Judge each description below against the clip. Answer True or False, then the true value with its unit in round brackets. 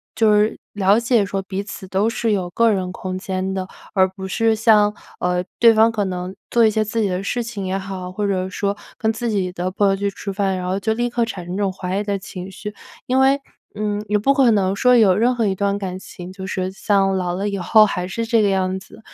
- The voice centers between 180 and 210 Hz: True (200 Hz)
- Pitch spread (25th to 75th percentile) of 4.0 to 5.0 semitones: False (2.7 semitones)